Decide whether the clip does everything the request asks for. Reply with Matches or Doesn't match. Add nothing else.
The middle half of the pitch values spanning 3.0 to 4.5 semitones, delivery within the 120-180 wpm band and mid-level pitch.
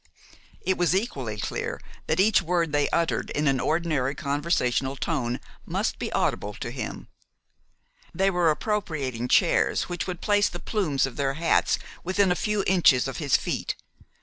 Doesn't match